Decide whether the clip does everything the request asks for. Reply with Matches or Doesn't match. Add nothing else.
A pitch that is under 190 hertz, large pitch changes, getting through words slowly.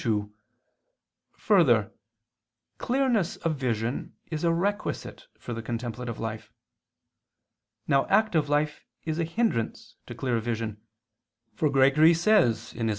Matches